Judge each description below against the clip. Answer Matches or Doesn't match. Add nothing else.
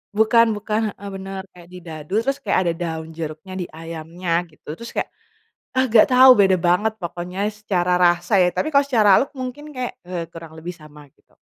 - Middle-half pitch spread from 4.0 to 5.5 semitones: Matches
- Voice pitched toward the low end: Doesn't match